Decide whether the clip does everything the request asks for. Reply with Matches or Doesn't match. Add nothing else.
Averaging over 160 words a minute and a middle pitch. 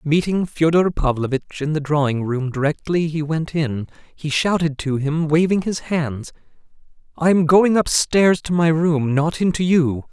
Matches